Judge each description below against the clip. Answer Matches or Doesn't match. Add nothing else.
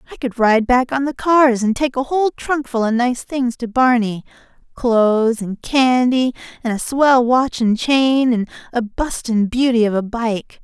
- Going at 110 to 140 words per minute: Doesn't match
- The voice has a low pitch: Doesn't match